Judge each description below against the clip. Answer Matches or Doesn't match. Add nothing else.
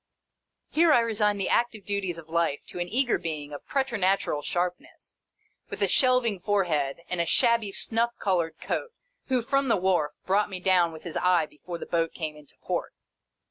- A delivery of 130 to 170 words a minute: Doesn't match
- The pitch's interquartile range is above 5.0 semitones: Matches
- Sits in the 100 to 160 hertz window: Doesn't match